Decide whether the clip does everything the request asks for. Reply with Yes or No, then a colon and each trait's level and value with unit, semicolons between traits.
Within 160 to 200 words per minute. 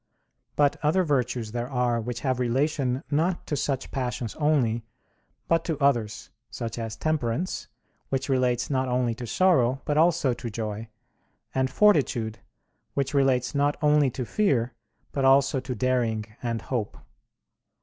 No: average, 145 wpm